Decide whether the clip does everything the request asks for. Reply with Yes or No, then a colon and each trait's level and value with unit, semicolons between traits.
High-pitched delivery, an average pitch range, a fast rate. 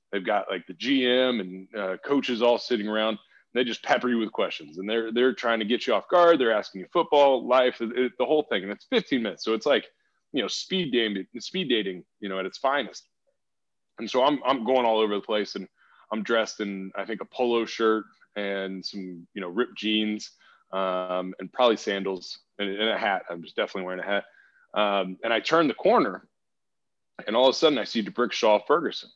No: low, 110 Hz; average, 4.3 semitones; fast, 220 wpm